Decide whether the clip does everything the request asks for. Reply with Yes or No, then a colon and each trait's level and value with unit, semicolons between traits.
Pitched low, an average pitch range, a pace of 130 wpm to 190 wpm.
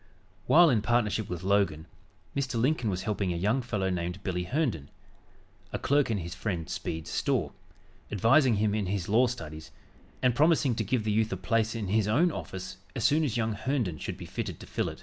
No: low, 110 Hz; average, 4.8 semitones; fast, 205 wpm